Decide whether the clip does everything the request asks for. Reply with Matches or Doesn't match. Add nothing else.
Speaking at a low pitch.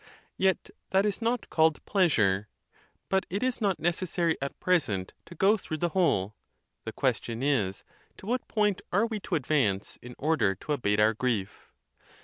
Doesn't match